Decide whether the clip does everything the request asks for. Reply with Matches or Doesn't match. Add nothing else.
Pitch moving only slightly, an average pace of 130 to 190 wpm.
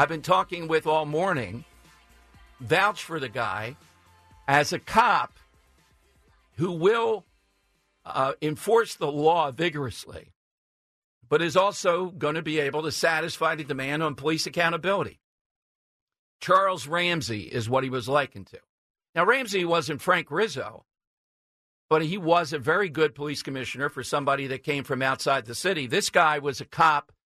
Doesn't match